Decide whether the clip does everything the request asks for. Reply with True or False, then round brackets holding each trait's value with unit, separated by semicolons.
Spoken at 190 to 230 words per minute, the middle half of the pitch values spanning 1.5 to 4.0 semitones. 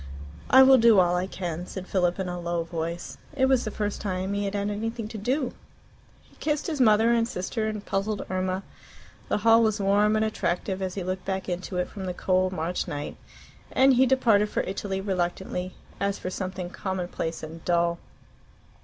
True (195 wpm; 3.2 semitones)